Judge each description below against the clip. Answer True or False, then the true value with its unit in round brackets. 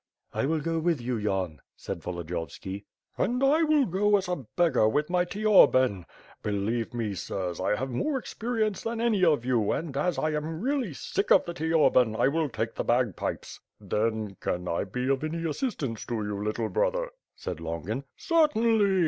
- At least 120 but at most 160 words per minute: False (180 wpm)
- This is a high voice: False (140 Hz)